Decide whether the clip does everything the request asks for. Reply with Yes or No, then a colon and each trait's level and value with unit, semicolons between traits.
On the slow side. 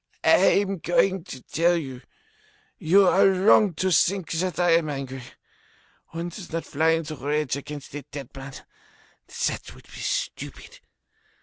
No: average, 160 wpm